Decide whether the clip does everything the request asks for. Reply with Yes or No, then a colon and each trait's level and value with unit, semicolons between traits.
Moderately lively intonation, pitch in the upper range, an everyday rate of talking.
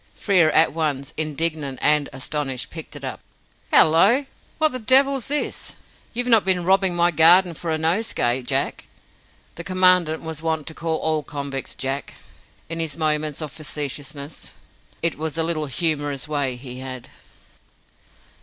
No: average, 3.4 semitones; medium, 160 Hz; average, 150 wpm